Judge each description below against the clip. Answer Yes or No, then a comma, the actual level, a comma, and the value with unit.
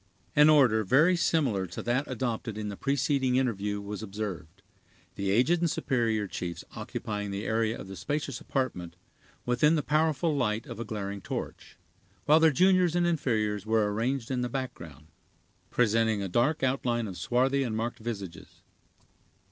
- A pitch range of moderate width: Yes, average, 5.0 semitones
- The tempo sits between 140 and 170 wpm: Yes, average, 160 wpm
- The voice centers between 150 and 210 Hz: No, low, 115 Hz